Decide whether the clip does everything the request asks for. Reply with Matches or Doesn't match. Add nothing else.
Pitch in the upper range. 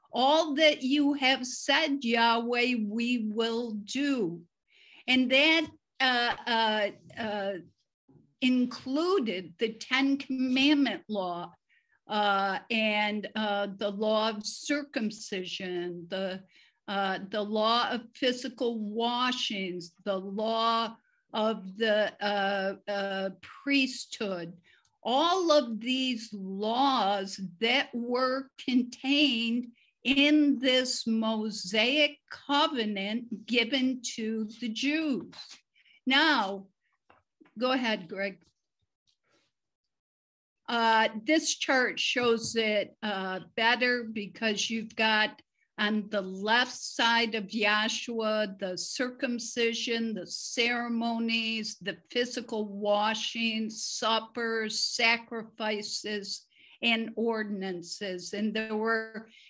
Matches